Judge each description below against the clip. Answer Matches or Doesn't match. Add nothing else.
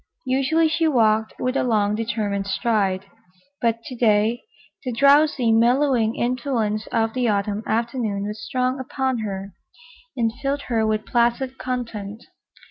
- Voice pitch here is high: Matches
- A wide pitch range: Doesn't match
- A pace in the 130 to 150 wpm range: Matches